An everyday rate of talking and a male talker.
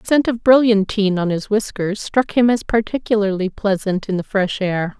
No: average, 190 wpm; female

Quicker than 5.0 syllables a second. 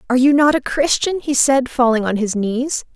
Yes: 5.2 syllables/s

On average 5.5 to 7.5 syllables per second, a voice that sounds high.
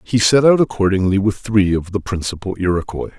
No: 5.6 syllables/s; low, 100 Hz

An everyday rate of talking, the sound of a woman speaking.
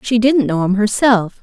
No: fast, 210 wpm; female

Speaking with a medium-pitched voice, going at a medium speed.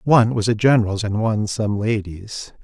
No: low, 110 Hz; average, 180 wpm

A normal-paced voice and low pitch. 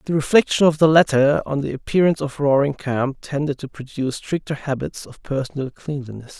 No: average, 180 wpm; medium, 145 Hz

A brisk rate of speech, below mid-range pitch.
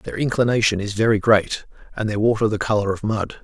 Yes: fast, 210 wpm; low, 110 Hz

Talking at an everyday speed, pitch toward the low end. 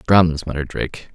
Yes: average, 155 wpm; very low, 80 Hz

